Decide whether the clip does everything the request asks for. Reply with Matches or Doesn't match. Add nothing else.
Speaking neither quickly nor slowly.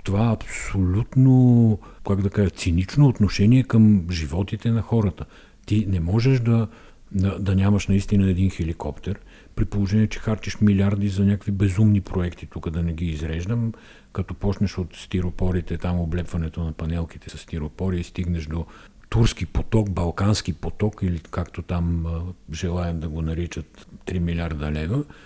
Matches